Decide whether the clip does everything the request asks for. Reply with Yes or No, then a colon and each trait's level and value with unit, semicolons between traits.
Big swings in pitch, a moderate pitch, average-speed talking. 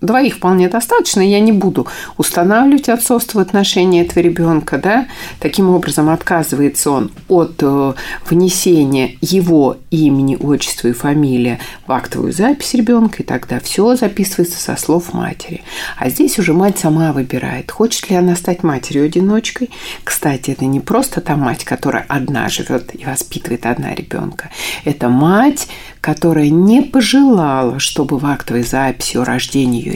Yes: wide, 6.4 semitones; medium, 170 Hz; average, 145 wpm